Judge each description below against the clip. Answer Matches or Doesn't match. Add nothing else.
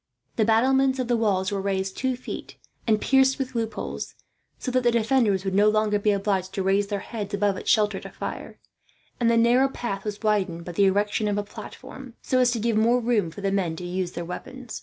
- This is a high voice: Matches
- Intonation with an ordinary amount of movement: Matches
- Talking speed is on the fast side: Matches